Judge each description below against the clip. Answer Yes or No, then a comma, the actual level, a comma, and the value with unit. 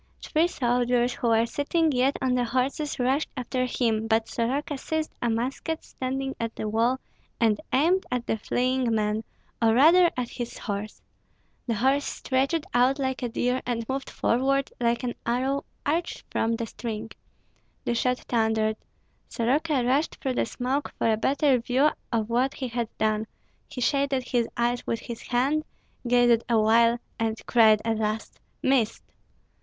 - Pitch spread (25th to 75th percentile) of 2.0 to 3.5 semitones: Yes, average, 2.8 semitones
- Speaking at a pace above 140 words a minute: Yes, average, 160 wpm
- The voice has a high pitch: Yes, high, 245 Hz